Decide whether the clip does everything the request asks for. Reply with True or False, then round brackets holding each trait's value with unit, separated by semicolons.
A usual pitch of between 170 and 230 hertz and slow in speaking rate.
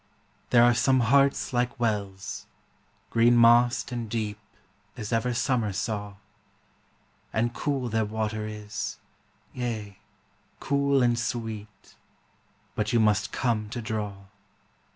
False (115 Hz; 115 wpm)